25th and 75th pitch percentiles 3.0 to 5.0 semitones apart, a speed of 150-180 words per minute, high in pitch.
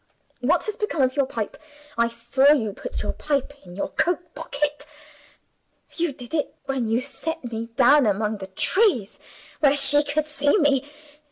Yes: average, 4.4 semitones; average, 170 wpm; very high, 280 Hz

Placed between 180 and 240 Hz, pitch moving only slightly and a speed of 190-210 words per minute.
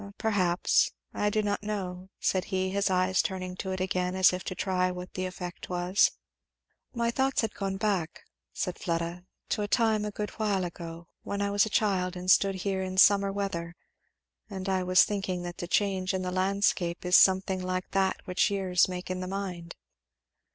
Yes: medium, 185 Hz; narrow, 1.7 semitones; average, 195 wpm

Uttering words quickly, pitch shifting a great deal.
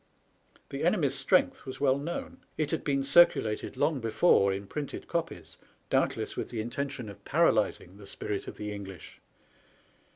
No: average, 160 wpm; wide, 5.8 semitones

